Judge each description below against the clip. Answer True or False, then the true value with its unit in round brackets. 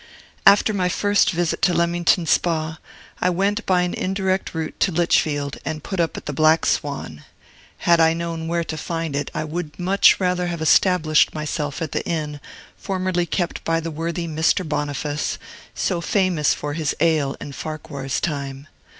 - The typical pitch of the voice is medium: True (165 Hz)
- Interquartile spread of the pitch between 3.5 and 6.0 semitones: False (2.7 semitones)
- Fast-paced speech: False (170 wpm)